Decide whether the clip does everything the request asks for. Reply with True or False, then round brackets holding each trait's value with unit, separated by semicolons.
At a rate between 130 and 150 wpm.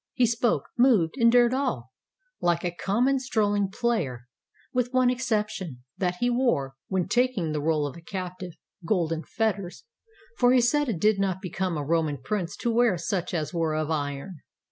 False (175 wpm)